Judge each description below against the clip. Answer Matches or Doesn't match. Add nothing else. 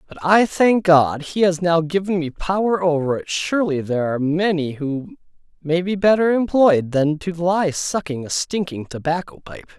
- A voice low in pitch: Doesn't match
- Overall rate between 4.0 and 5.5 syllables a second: Matches